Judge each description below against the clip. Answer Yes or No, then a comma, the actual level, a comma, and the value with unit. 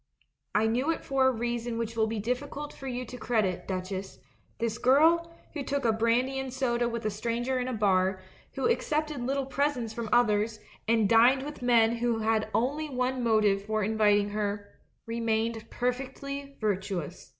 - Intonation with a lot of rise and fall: No, average, 3.3 semitones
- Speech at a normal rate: Yes, average, 180 wpm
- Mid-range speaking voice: No, high, 235 Hz